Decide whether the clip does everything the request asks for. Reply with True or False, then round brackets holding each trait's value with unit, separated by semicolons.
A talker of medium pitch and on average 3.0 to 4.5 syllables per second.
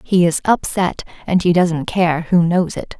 True (175 Hz; 4.2 syllables/s)